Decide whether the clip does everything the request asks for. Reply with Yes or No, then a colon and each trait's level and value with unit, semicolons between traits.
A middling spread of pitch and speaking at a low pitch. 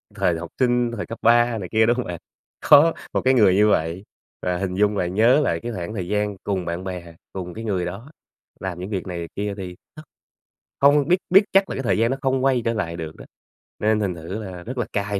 Yes: average, 4.9 semitones; low, 105 Hz